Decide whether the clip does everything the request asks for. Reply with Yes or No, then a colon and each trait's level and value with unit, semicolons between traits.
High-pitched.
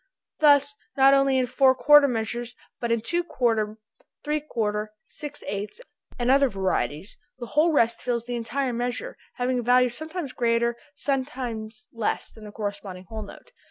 Yes: high, 245 Hz